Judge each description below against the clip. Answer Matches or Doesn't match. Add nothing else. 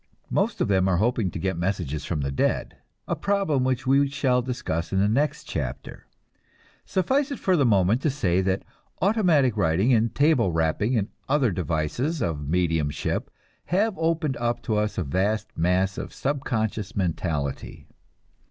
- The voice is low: Matches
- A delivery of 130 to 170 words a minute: Matches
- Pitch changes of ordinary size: Doesn't match